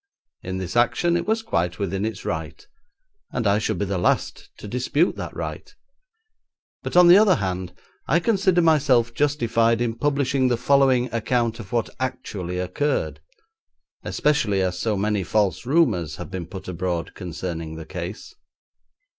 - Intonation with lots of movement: Yes, wide, 7.2 semitones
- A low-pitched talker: Yes, low, 115 Hz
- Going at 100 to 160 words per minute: Yes, average, 155 wpm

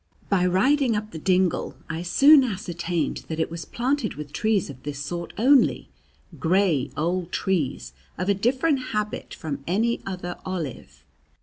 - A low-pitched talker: No, medium, 185 Hz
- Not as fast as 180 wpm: Yes, average, 150 wpm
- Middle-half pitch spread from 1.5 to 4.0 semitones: No, average, 5.1 semitones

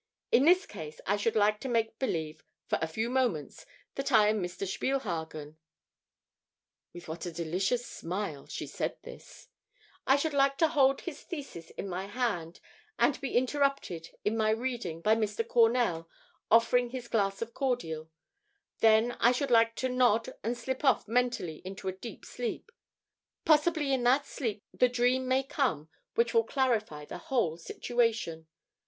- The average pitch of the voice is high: Yes, high, 230 Hz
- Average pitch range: No, wide, 6.0 semitones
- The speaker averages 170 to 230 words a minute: No, average, 160 wpm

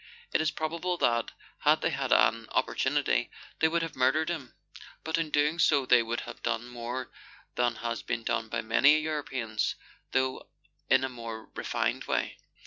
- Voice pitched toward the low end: Yes, low, 130 Hz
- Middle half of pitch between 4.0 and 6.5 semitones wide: Yes, average, 4.9 semitones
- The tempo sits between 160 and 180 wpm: Yes, average, 170 wpm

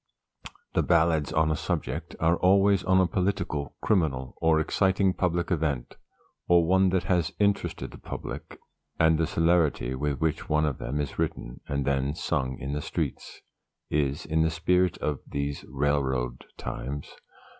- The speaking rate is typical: Yes, average, 155 wpm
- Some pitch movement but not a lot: Yes, average, 3.8 semitones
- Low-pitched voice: Yes, very low, 80 Hz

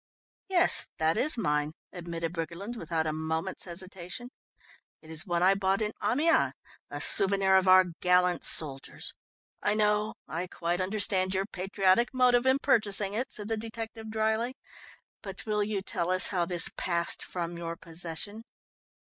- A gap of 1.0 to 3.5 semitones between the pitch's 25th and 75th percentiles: No, average, 4.0 semitones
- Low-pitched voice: No, high, 190 Hz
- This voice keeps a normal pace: Yes, average, 160 wpm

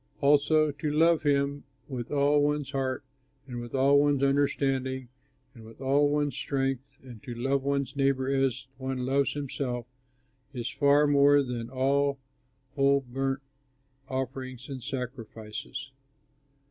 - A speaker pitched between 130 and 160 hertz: Yes, low, 135 Hz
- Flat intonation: Yes, narrow, 1.5 semitones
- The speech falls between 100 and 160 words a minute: Yes, slow, 135 wpm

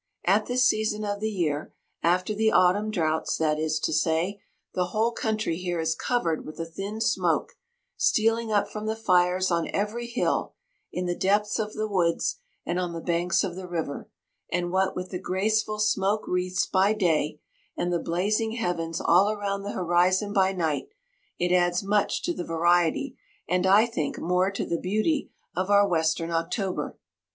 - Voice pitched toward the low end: No, medium, 185 Hz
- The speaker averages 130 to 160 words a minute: No, average, 175 wpm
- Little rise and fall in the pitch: No, average, 3.5 semitones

